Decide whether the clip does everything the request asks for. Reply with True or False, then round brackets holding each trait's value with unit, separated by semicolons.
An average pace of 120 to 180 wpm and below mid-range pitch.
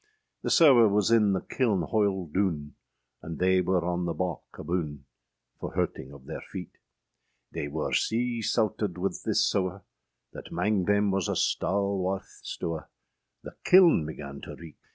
True (160 wpm; 95 Hz)